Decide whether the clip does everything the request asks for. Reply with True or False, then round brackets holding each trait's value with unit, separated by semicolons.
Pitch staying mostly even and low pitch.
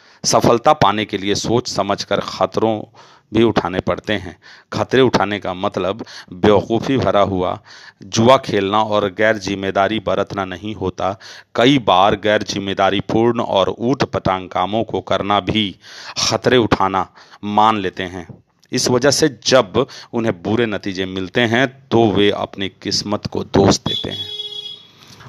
False (3.2 semitones; 105 Hz)